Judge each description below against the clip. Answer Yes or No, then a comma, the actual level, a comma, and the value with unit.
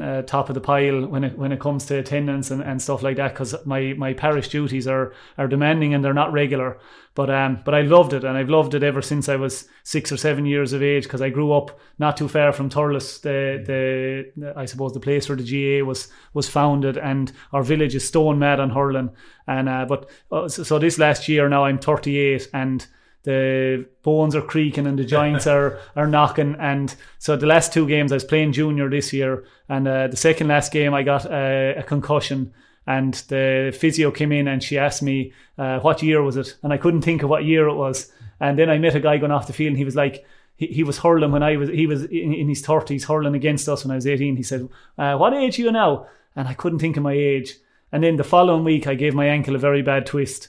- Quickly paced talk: Yes, fast, 245 wpm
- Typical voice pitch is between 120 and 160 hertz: Yes, medium, 140 Hz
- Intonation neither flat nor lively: No, narrow, 1.8 semitones